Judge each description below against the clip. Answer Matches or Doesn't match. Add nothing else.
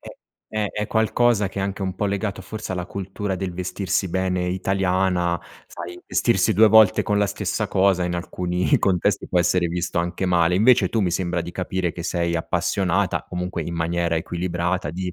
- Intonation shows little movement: Matches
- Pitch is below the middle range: Matches